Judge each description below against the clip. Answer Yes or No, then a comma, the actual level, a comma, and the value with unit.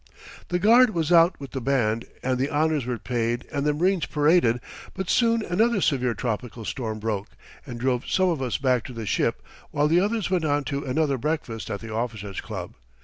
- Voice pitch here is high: No, medium, 140 Hz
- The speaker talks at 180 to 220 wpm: Yes, average, 200 wpm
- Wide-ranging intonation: Yes, wide, 6.0 semitones